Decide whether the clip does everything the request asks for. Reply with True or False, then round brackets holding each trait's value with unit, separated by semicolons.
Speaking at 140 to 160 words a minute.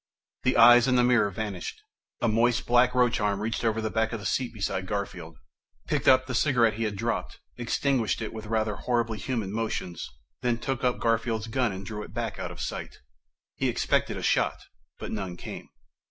False (195 wpm)